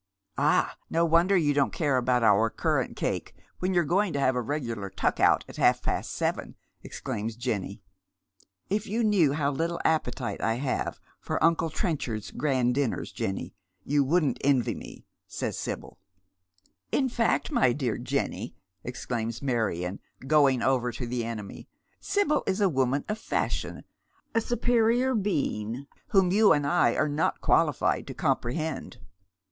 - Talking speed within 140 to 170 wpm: Yes, average, 165 wpm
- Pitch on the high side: No, medium, 140 Hz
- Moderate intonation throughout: No, wide, 6.5 semitones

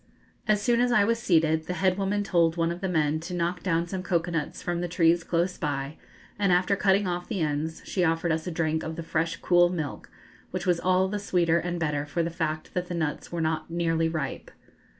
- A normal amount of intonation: No, narrow, 2.2 semitones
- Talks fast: Yes, fast, 235 wpm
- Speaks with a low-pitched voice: No, medium, 170 Hz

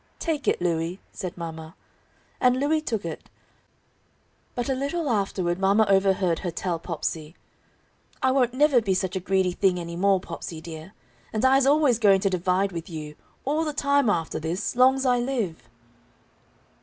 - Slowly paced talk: No, average, 165 wpm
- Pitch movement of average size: No, wide, 7.0 semitones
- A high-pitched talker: Yes, high, 195 Hz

